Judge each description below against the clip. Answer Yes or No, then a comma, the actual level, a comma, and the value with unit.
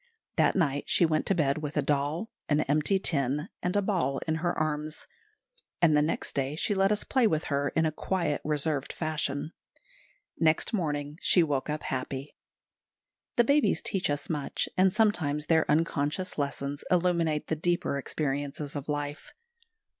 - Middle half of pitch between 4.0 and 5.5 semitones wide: No, average, 3.2 semitones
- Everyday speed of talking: Yes, average, 160 wpm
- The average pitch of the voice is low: No, medium, 155 Hz